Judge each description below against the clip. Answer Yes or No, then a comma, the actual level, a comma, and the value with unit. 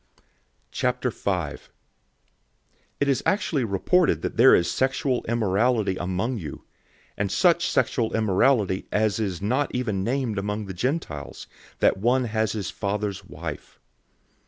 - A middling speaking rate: No, slow, 125 wpm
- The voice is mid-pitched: No, low, 110 Hz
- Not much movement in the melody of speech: No, average, 4.7 semitones